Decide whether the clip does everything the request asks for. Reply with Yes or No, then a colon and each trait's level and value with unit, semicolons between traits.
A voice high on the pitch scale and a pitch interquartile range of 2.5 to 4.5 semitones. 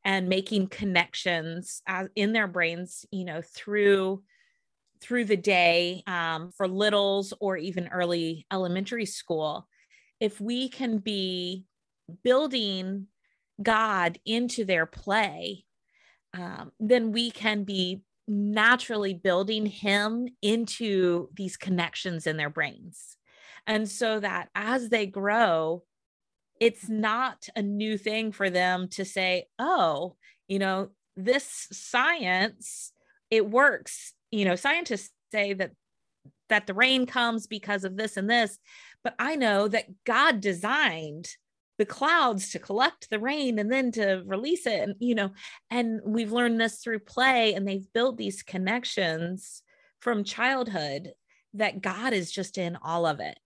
Yes: high, 205 Hz; average, 3.5 semitones